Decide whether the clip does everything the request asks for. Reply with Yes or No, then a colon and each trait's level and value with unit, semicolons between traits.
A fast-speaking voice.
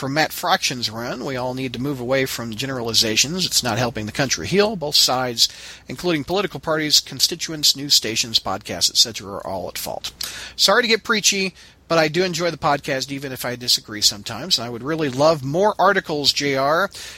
No: average, 190 wpm